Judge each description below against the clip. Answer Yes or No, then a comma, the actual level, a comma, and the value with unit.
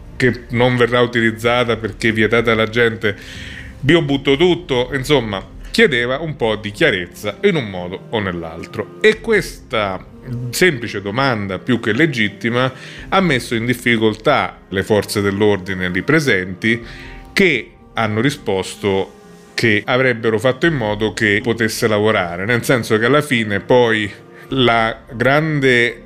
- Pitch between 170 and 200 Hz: No, low, 115 Hz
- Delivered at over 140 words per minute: No, average, 130 wpm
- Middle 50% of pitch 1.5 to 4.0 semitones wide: Yes, average, 3.5 semitones